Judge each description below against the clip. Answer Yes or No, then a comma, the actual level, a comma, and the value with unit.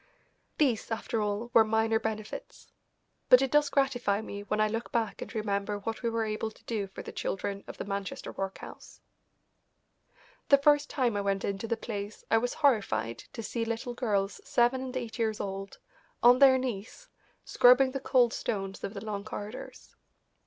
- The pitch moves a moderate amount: Yes, average, 3.4 semitones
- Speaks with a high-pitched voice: Yes, high, 225 Hz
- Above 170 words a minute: Yes, average, 180 wpm